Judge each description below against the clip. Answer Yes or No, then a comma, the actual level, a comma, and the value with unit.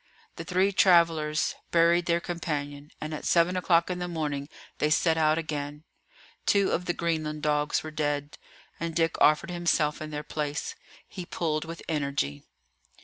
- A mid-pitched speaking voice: Yes, medium, 155 Hz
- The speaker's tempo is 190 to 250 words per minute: No, average, 160 wpm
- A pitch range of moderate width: No, narrow, 2.3 semitones